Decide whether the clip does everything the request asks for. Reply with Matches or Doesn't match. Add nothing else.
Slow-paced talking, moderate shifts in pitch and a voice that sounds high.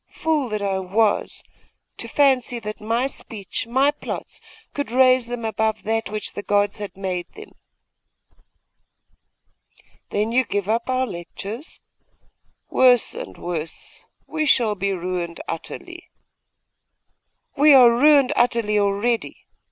Matches